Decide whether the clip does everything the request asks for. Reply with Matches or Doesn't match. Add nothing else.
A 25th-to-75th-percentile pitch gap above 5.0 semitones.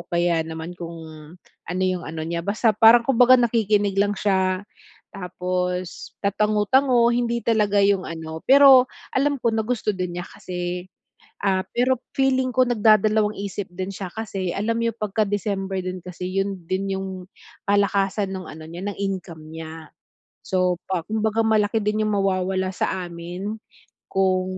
Doesn't match